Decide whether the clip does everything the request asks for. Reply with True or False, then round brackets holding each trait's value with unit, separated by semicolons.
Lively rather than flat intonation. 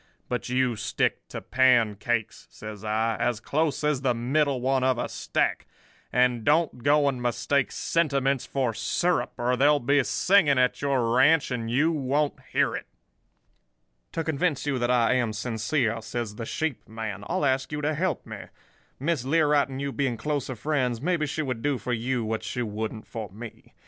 False (3.8 semitones)